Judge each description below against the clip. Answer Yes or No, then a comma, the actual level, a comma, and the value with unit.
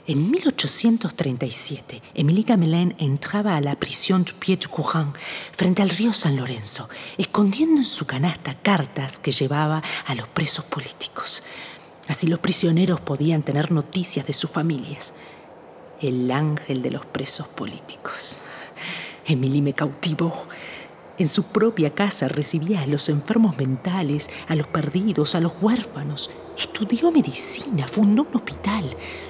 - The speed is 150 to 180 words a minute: No, average, 130 wpm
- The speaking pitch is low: No, medium, 165 Hz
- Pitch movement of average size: Yes, average, 4.9 semitones